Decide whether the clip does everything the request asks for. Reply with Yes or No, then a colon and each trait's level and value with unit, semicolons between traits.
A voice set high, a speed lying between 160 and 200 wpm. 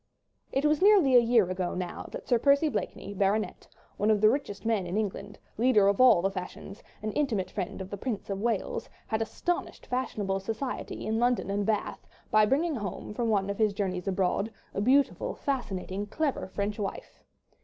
Yes: high, 215 Hz; average, 185 wpm